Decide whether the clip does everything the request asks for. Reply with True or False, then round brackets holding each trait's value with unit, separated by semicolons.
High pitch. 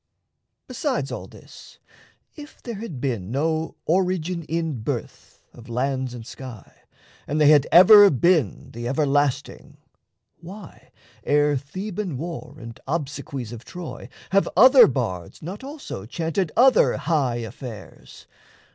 False (150 Hz)